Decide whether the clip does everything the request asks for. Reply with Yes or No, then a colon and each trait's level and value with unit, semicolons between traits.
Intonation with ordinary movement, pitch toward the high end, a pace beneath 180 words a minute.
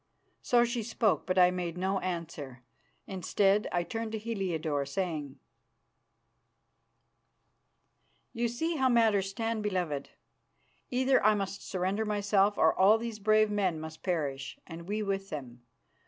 Yes: average, 4.3 semitones; high, 195 Hz; slow, 135 wpm